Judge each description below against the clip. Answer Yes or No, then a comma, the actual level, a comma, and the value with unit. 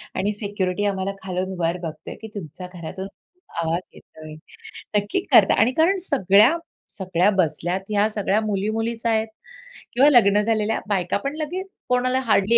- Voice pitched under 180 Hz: No, high, 205 Hz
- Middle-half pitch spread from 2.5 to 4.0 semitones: Yes, average, 3.7 semitones